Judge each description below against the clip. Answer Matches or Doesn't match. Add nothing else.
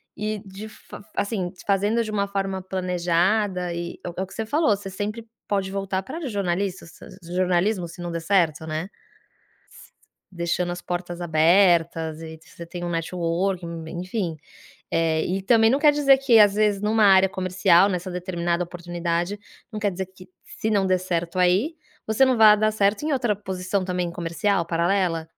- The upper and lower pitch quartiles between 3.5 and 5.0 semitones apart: Doesn't match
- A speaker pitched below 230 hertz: Matches